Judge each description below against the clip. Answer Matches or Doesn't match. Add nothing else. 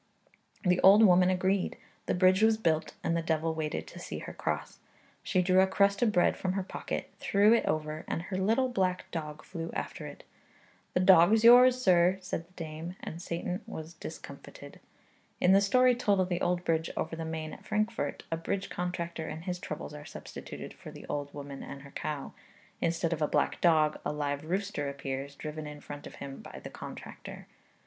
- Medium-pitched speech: Matches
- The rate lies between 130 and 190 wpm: Doesn't match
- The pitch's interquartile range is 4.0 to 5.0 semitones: Doesn't match